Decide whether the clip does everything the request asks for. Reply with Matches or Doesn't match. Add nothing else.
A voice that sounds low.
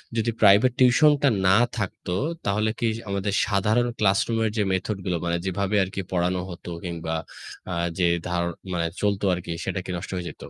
Matches